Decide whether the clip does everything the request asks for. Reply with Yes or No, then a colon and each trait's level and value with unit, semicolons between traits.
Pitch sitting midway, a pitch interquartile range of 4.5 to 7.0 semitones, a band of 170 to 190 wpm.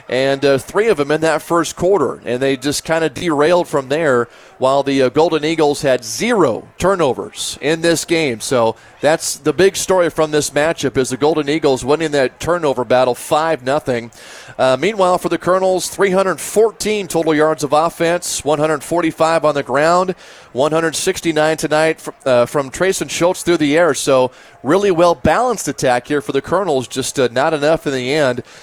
No: medium, 155 Hz; average, 3.8 semitones; average, 180 wpm